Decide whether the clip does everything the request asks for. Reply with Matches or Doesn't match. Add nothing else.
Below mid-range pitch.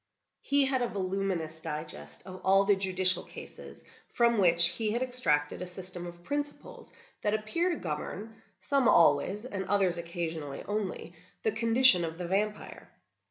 Doesn't match